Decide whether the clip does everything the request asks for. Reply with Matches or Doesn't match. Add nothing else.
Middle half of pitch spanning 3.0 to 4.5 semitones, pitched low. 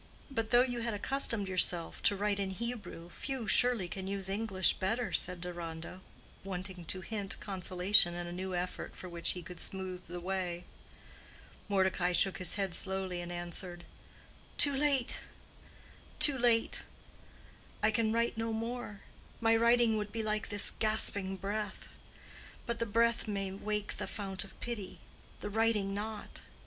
Doesn't match